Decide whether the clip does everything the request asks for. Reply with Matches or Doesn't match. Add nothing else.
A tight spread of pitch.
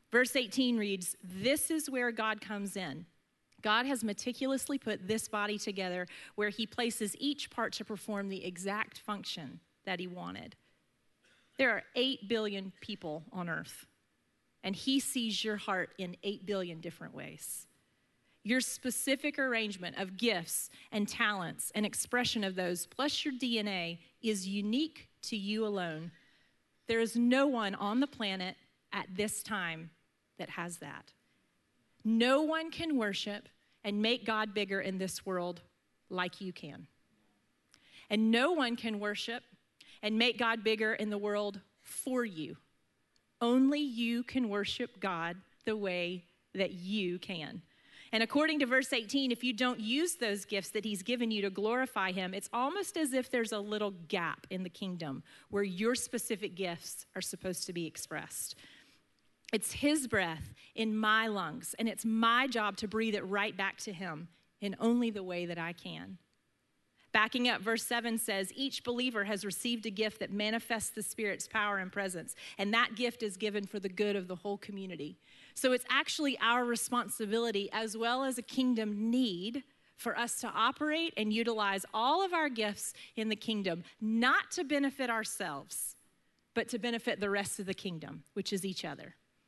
Doesn't match